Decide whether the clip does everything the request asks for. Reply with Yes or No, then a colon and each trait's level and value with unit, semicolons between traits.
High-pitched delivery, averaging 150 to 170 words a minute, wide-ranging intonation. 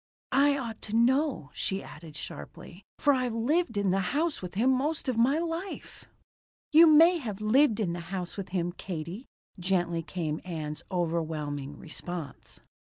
Yes: high, 195 Hz; average, 160 wpm; wide, 8.0 semitones